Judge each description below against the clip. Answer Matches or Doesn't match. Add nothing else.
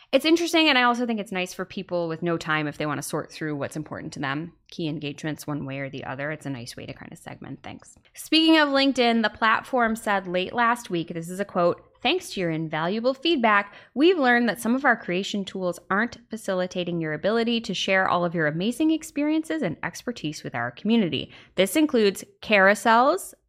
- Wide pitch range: Matches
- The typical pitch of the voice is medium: Doesn't match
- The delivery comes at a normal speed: Doesn't match